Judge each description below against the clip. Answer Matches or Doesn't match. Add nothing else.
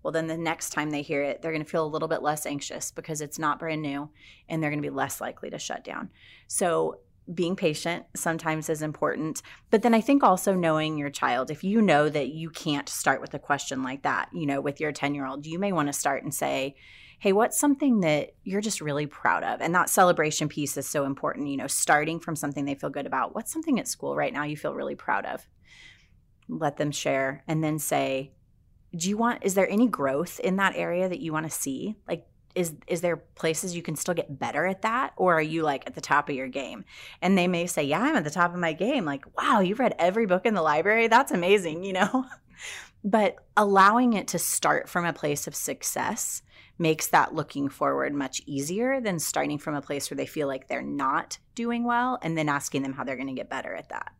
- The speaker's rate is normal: Doesn't match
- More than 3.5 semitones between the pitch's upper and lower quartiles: Matches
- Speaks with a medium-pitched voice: Matches